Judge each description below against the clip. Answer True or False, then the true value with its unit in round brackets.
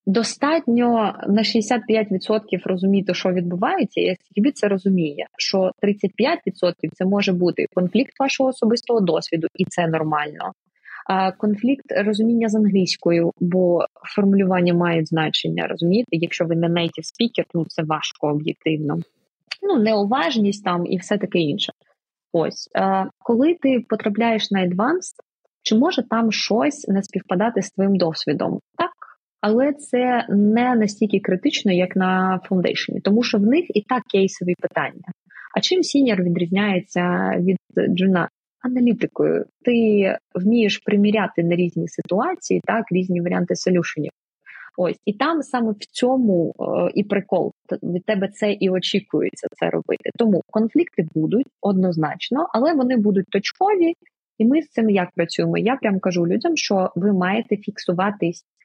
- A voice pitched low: False (200 Hz)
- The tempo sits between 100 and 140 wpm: True (135 wpm)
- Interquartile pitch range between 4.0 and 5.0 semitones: True (4.3 semitones)